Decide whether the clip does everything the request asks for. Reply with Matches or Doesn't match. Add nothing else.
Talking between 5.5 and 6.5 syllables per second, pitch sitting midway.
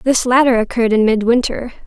Doesn't match